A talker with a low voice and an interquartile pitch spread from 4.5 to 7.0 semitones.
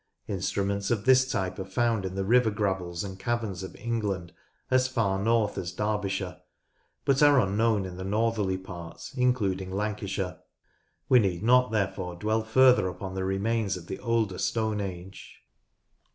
No: low, 100 Hz; average, 3.3 semitones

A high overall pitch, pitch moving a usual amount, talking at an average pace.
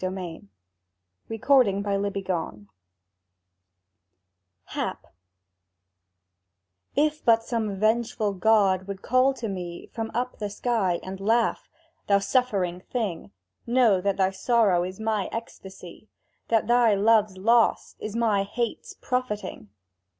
No: high, 210 Hz; average, 3.3 semitones; slow, 115 wpm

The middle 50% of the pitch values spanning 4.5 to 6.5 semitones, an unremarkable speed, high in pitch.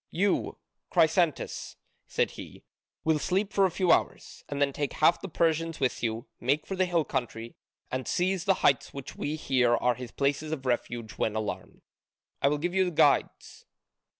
No: wide, 5.5 semitones; average, 175 wpm; medium, 150 Hz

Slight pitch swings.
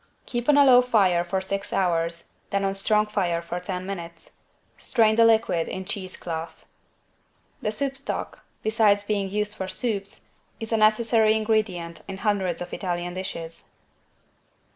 No: average, 3.5 semitones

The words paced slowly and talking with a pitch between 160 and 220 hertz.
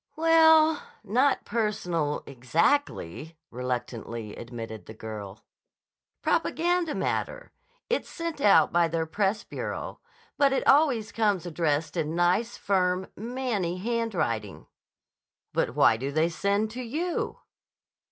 Yes: slow, 115 wpm; high, 190 Hz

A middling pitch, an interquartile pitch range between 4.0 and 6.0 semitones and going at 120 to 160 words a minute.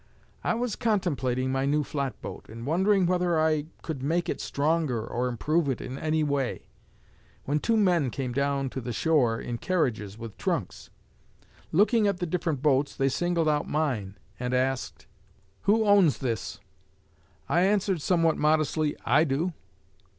Yes: medium, 150 Hz; average, 4.9 semitones; average, 155 wpm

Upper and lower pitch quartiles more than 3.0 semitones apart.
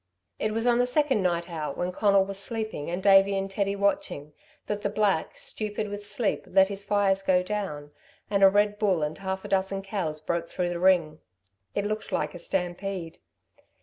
No: narrow, 2.6 semitones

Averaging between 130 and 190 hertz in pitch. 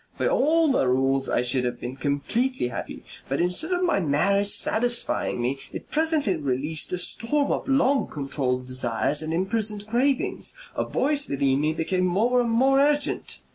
Yes: medium, 185 Hz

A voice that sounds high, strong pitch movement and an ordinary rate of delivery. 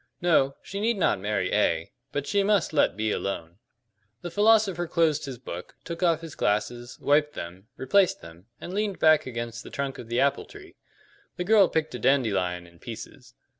No: medium, 140 Hz; wide, 8.9 semitones; average, 185 wpm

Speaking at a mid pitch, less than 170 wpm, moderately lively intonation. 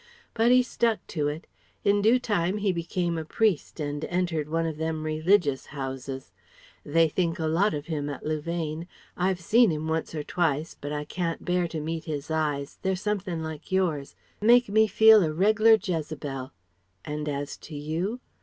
No: medium, 165 Hz; average, 180 wpm; average, 4.0 semitones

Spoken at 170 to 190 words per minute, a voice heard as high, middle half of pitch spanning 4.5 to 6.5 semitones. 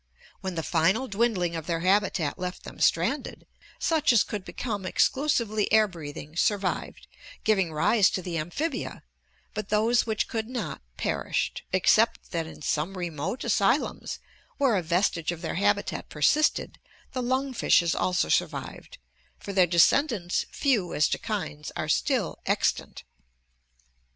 No: average, 140 wpm; high, 195 Hz; average, 5.0 semitones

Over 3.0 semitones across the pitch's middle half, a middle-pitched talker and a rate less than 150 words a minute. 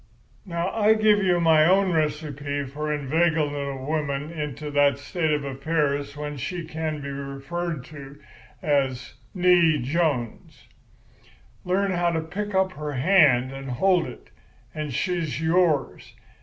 Yes: average, 3.5 semitones; medium, 155 Hz; average, 140 wpm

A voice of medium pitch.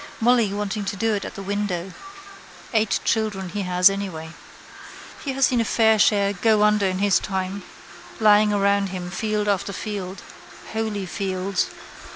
No: high, 200 Hz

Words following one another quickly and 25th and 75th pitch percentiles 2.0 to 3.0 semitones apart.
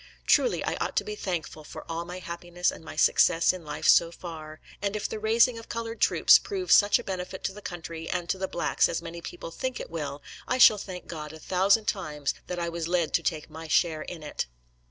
No: fast, 235 wpm; average, 3.7 semitones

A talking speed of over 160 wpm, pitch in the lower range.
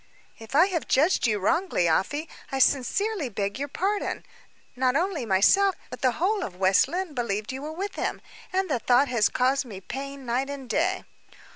No: average, 185 wpm; very high, 275 Hz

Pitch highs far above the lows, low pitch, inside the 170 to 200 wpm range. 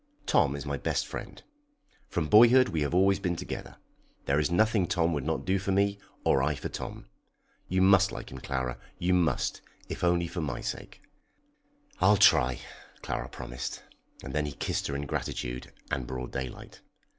Yes: wide, 6.1 semitones; very low, 80 Hz; average, 180 wpm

